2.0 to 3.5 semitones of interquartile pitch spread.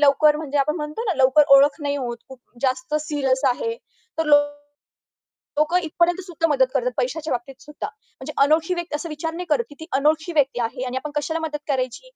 Yes: average, 3.2 semitones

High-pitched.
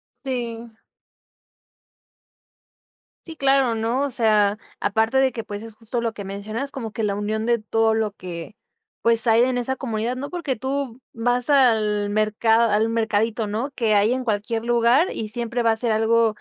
Yes: high, 230 Hz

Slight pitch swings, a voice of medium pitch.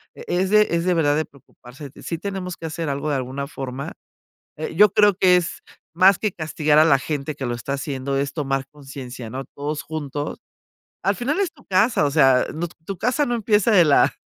No: average, 5.3 semitones; medium, 155 Hz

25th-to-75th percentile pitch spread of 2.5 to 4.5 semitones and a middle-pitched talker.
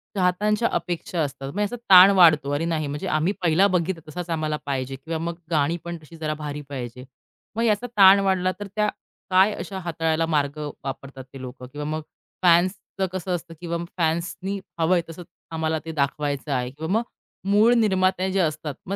Yes: average, 3.9 semitones; medium, 165 Hz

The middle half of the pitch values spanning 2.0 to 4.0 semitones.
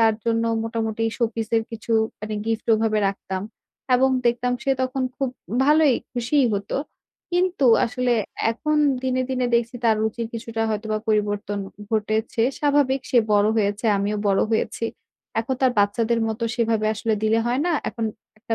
Yes: narrow, 2.6 semitones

